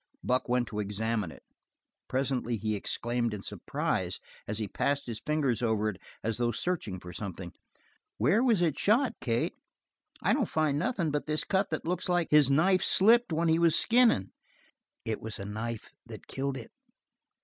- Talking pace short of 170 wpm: No, average, 175 wpm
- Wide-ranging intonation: Yes, wide, 7.2 semitones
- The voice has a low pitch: Yes, low, 130 Hz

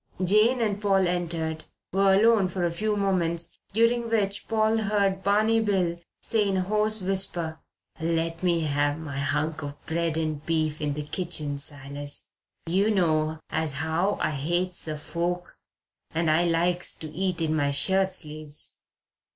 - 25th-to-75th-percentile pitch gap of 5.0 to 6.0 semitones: No, average, 3.9 semitones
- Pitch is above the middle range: No, medium, 170 Hz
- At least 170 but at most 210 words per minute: No, average, 160 wpm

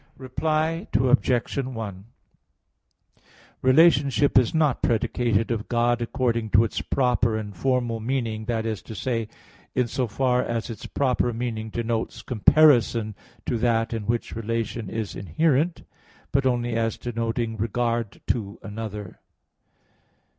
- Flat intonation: Yes, narrow, 2.3 semitones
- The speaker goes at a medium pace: No, slow, 125 wpm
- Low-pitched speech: Yes, low, 120 Hz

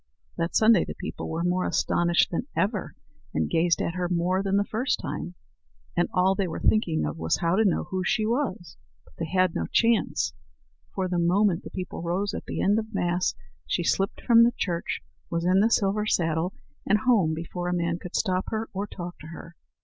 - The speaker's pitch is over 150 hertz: Yes, medium, 185 Hz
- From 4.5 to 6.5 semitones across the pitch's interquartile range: No, average, 3.1 semitones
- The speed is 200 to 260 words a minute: Yes, fast, 205 wpm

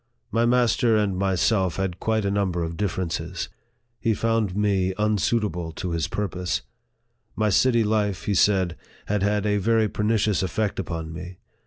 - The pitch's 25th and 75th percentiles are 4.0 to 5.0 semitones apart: No, average, 2.9 semitones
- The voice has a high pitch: No, low, 100 Hz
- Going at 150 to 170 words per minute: Yes, average, 160 wpm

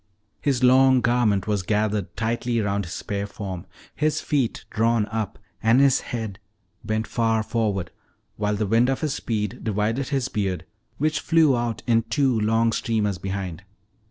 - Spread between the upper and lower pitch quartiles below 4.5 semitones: Yes, average, 3.1 semitones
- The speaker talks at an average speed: Yes, average, 155 wpm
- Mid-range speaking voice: No, low, 110 Hz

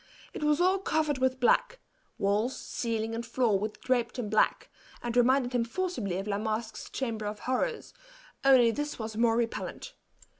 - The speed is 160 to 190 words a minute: Yes, average, 165 wpm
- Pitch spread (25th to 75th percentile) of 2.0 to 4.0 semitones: Yes, average, 3.6 semitones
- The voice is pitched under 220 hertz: No, high, 240 Hz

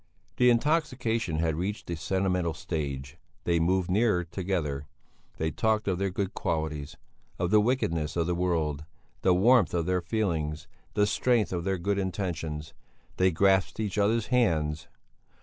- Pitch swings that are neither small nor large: Yes, average, 4.2 semitones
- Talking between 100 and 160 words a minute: Yes, average, 150 wpm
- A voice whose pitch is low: Yes, very low, 90 Hz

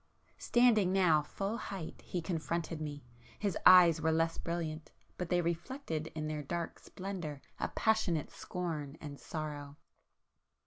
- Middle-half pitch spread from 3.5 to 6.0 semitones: No, average, 3.0 semitones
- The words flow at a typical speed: No, slow, 130 wpm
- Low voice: No, medium, 165 Hz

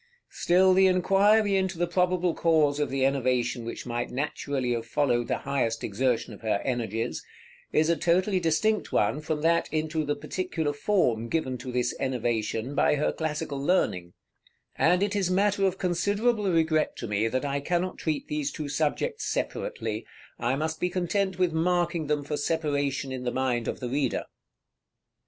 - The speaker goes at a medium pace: Yes, average, 170 wpm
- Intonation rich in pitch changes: Yes, wide, 5.8 semitones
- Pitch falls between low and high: Yes, medium, 150 Hz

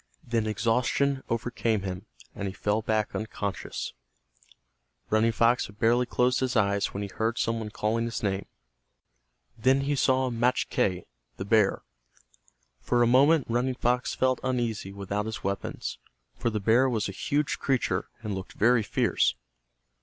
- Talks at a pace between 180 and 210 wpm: No, average, 155 wpm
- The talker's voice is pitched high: No, low, 115 Hz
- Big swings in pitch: No, average, 3.2 semitones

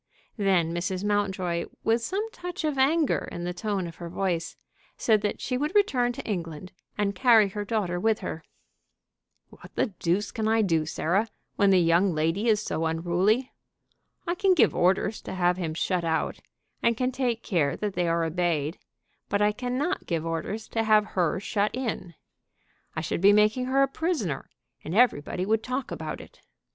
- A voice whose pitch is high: Yes, high, 200 Hz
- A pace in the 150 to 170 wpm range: No, average, 180 wpm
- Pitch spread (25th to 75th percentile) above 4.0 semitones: Yes, average, 5.1 semitones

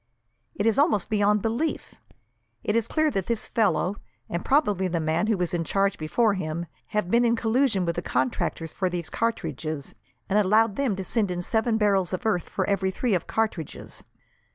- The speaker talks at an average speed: Yes, average, 190 wpm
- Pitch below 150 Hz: No, high, 200 Hz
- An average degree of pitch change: Yes, average, 4.2 semitones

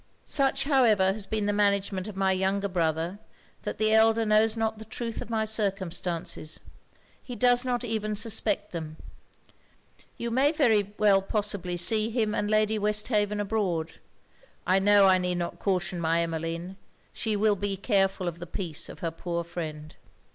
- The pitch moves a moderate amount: Yes, average, 3.4 semitones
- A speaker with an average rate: Yes, average, 160 wpm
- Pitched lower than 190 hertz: No, high, 205 Hz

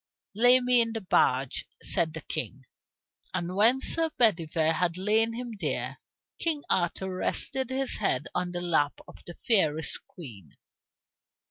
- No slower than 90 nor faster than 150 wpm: Yes, average, 145 wpm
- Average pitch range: No, wide, 6.4 semitones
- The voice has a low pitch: No, medium, 180 Hz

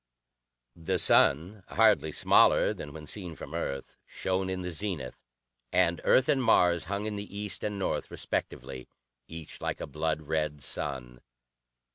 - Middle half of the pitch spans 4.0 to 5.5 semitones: Yes, average, 5.1 semitones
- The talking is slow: No, average, 150 wpm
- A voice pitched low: Yes, very low, 85 Hz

